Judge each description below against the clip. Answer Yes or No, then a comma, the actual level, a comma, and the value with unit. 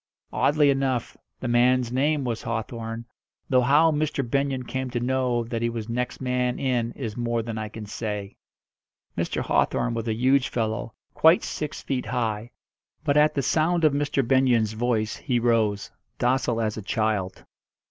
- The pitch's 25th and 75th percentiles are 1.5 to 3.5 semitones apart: Yes, average, 2.9 semitones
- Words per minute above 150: Yes, average, 170 wpm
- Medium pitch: No, low, 120 Hz